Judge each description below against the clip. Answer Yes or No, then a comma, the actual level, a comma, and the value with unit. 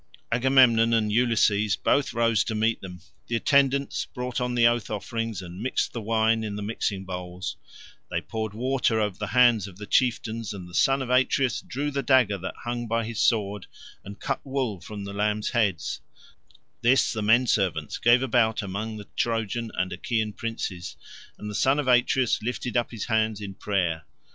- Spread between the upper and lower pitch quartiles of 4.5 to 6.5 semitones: No, average, 3.1 semitones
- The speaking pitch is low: Yes, low, 110 Hz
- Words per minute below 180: No, average, 185 wpm